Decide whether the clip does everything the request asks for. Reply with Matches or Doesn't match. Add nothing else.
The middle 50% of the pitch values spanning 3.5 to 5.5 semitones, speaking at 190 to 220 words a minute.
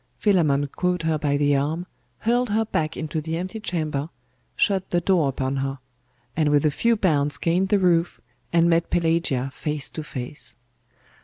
Doesn't match